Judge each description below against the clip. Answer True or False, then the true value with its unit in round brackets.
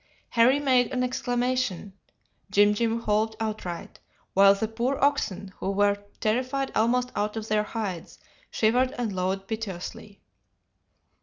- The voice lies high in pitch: True (220 Hz)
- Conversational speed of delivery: False (130 wpm)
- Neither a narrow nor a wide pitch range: True (3.5 semitones)